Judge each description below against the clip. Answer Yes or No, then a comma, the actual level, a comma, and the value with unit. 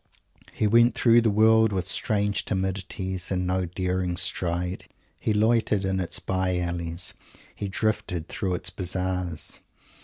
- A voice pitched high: No, very low, 95 Hz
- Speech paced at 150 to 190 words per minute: No, average, 140 wpm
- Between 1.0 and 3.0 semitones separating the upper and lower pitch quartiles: Yes, narrow, 2.4 semitones